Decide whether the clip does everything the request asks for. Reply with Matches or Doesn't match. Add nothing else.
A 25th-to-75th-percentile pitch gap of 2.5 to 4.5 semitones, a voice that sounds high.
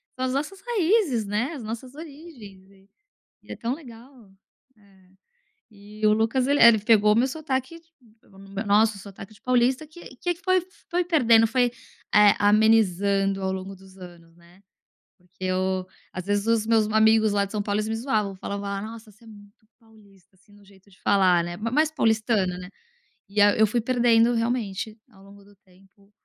Matches